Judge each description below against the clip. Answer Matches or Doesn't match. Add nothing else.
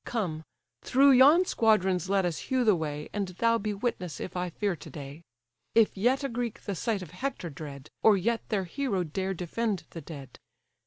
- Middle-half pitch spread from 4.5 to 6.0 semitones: Matches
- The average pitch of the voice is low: Doesn't match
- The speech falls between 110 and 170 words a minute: Doesn't match